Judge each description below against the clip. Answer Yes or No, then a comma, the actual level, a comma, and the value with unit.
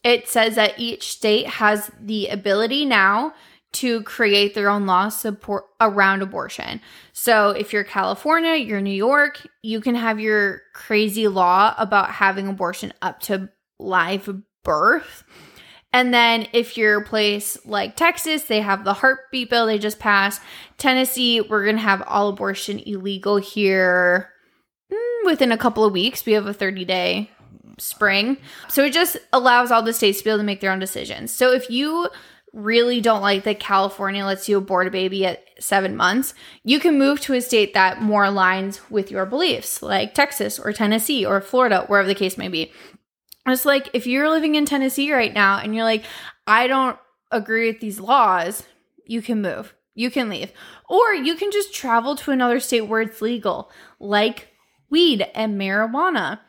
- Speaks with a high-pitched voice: Yes, high, 215 Hz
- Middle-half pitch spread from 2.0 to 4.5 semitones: Yes, average, 4.2 semitones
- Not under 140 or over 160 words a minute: No, average, 175 wpm